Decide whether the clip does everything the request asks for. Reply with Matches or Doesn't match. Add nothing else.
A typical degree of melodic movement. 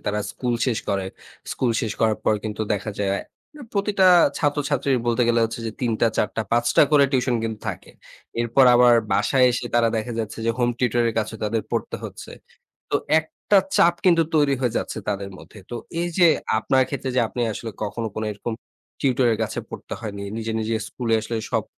Matches